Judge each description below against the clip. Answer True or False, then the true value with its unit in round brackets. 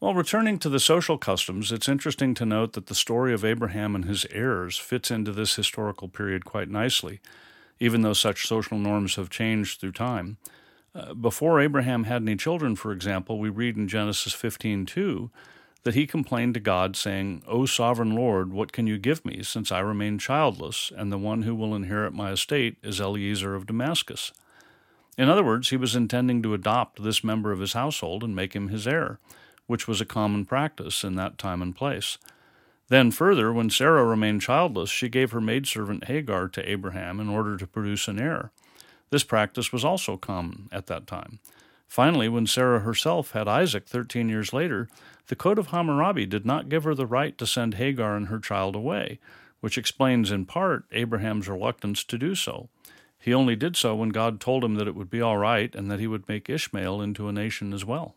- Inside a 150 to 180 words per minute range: False (200 wpm)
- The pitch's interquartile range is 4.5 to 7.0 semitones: False (3.4 semitones)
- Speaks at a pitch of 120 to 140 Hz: False (110 Hz)